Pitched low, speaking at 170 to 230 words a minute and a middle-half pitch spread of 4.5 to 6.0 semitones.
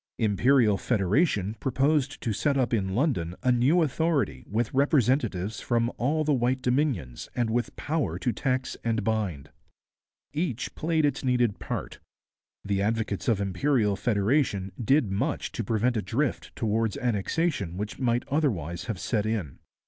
No: low, 120 Hz; average, 150 wpm; average, 5.0 semitones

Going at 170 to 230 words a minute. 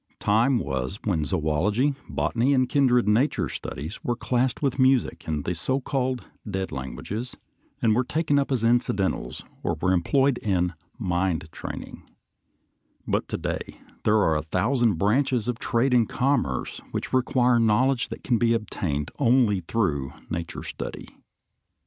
No: average, 150 wpm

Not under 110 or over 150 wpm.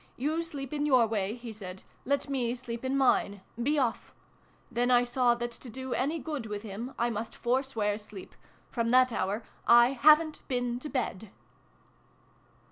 No: average, 190 wpm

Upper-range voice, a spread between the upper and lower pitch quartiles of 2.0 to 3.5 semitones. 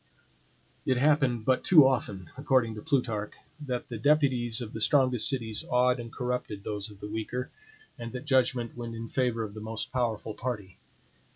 No: low, 120 Hz; average, 2.8 semitones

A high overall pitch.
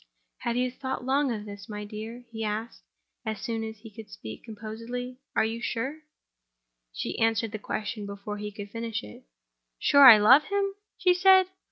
Yes: high, 225 Hz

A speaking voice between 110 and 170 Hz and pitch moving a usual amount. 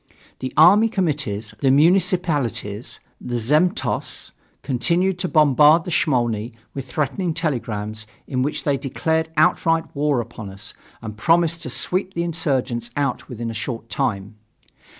No: medium, 140 Hz; wide, 5.9 semitones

